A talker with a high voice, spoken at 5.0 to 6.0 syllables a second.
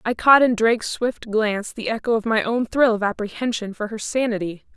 Yes: high, 225 Hz; 5.5 syllables/s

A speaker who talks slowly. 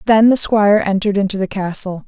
No: fast, 205 wpm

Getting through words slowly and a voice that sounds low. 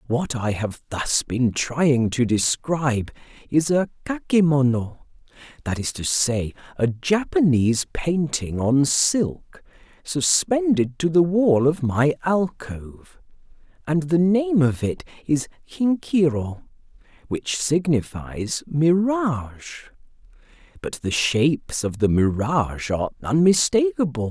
No: slow, 105 wpm; medium, 145 Hz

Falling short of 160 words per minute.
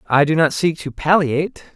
No: fast, 205 wpm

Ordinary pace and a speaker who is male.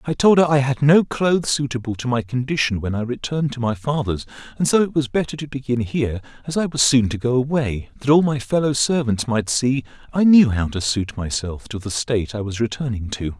No: fast, 235 wpm; male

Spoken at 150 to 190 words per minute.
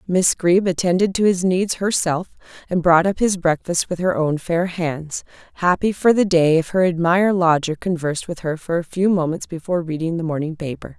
No: average, 200 wpm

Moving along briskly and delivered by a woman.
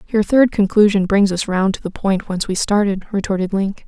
Yes: fast, 215 wpm; female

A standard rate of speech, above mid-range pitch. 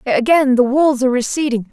Yes: average, 175 wpm; very high, 260 Hz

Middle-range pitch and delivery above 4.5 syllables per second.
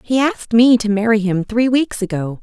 No: high, 220 Hz; 5.2 syllables/s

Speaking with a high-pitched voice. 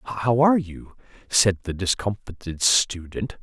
No: low, 105 Hz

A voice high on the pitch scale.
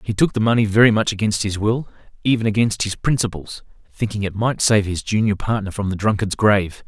No: low, 105 Hz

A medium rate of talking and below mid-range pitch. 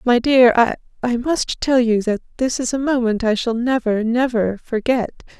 No: average, 180 wpm; high, 240 Hz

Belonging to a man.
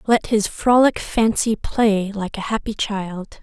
No: female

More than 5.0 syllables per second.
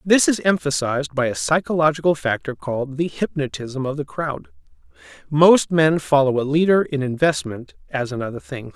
Yes: 5.2 syllables/s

